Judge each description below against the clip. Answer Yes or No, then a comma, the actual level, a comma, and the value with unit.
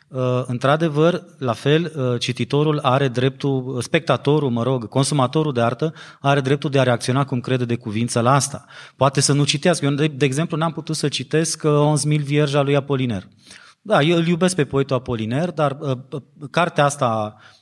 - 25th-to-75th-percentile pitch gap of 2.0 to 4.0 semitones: Yes, average, 3.2 semitones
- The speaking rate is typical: No, fast, 180 wpm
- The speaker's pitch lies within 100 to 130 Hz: No, medium, 140 Hz